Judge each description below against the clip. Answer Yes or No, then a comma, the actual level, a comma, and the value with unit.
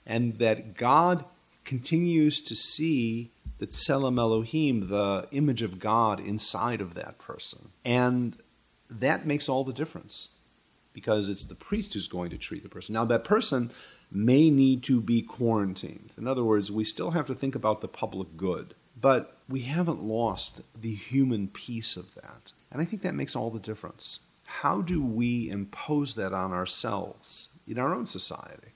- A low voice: Yes, low, 115 Hz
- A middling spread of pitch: Yes, average, 4.2 semitones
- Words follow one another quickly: No, average, 170 wpm